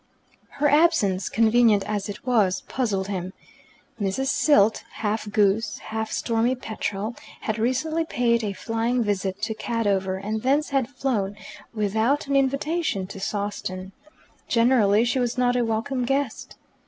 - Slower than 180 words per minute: Yes, average, 140 wpm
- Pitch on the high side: Yes, high, 225 Hz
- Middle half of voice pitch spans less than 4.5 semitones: Yes, average, 3.9 semitones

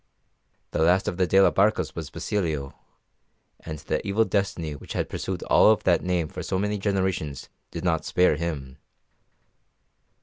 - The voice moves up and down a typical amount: Yes, average, 3.7 semitones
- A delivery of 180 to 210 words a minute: No, average, 165 wpm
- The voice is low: Yes, very low, 90 Hz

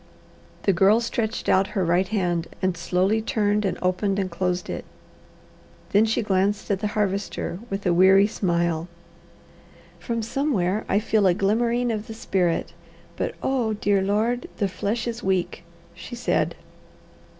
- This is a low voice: No, high, 200 Hz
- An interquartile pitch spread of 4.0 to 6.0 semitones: No, average, 3.1 semitones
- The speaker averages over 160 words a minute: No, average, 150 wpm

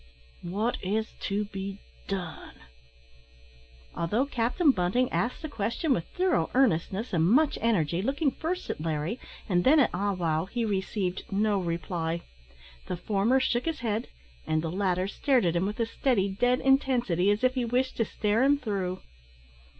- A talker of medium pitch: No, high, 210 Hz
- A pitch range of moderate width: No, wide, 5.7 semitones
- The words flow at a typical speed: Yes, average, 165 wpm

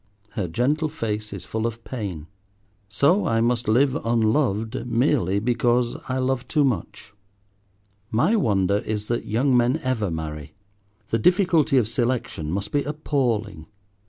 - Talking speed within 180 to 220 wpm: No, average, 140 wpm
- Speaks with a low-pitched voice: Yes, low, 115 Hz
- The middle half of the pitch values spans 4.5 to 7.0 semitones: No, average, 4.0 semitones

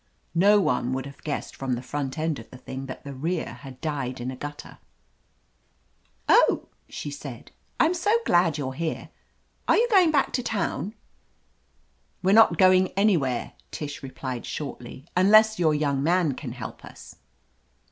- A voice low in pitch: No, medium, 150 Hz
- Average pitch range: No, wide, 6.1 semitones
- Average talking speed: Yes, average, 165 wpm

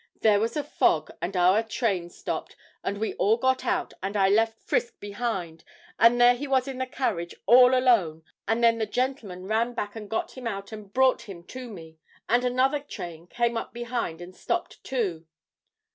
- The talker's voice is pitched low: No, high, 225 Hz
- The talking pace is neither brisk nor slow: Yes, average, 190 wpm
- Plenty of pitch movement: No, average, 4.4 semitones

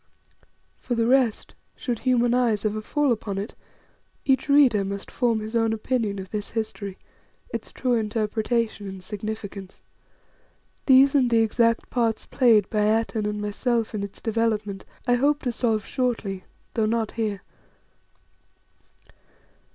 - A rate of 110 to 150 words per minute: Yes, average, 140 wpm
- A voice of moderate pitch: No, high, 225 Hz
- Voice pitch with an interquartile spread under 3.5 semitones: Yes, narrow, 2.6 semitones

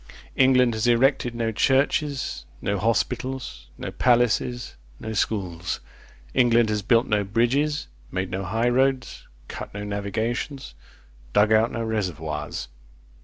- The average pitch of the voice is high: No, low, 115 Hz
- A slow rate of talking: Yes, slow, 120 wpm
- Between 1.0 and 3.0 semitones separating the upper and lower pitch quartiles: No, average, 3.7 semitones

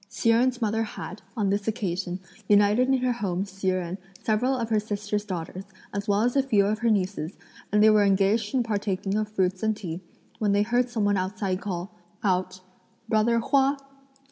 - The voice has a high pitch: Yes, high, 205 Hz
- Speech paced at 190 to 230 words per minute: Yes, average, 195 wpm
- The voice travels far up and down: No, average, 2.7 semitones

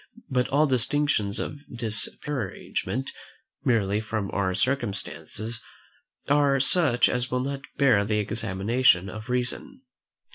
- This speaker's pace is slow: Yes, slow, 110 wpm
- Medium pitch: No, low, 120 Hz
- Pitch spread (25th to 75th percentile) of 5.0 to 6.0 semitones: No, average, 4.6 semitones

